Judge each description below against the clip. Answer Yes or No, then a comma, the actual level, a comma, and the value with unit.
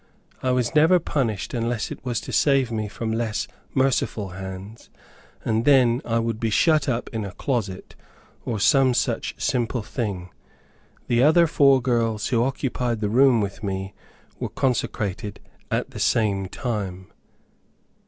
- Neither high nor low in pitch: No, low, 115 Hz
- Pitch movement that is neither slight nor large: Yes, average, 3.8 semitones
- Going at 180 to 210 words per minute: No, average, 150 wpm